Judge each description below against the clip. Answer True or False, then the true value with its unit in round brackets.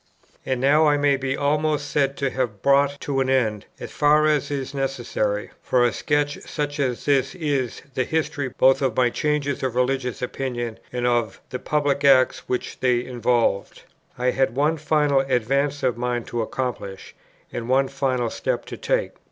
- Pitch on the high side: False (135 Hz)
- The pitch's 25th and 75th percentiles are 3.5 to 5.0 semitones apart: False (2.6 semitones)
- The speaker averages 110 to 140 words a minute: False (175 wpm)